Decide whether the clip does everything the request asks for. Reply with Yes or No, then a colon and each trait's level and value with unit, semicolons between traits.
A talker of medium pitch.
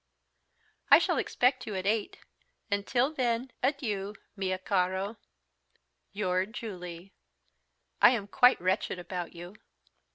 No: high, 200 Hz